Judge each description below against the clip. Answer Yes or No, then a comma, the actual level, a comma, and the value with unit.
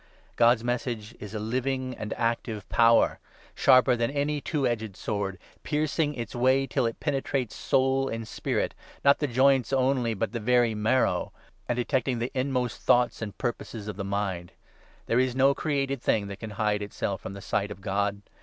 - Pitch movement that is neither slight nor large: Yes, average, 3.7 semitones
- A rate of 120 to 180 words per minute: No, average, 190 wpm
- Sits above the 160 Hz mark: No, low, 120 Hz